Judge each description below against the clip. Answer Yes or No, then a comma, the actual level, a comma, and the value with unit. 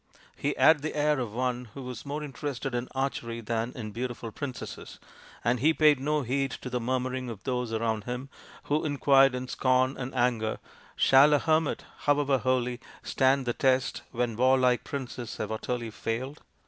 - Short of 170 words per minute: No, average, 175 wpm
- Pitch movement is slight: Yes, narrow, 2.3 semitones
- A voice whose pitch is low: Yes, low, 130 Hz